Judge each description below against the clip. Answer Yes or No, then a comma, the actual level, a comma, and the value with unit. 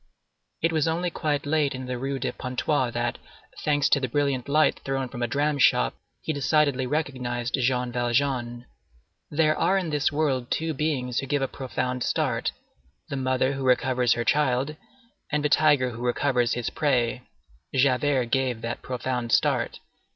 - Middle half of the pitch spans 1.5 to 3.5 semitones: Yes, average, 2.9 semitones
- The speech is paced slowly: No, average, 165 wpm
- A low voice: Yes, low, 130 Hz